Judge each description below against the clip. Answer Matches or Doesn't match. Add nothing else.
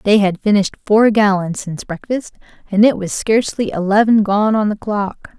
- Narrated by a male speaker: Doesn't match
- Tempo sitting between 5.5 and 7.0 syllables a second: Doesn't match